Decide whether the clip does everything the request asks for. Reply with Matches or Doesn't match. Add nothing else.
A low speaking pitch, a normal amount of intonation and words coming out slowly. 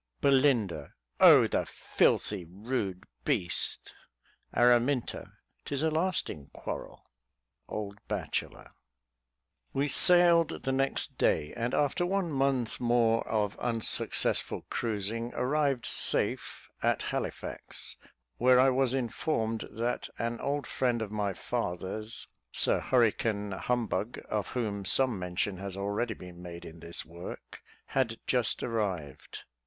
Matches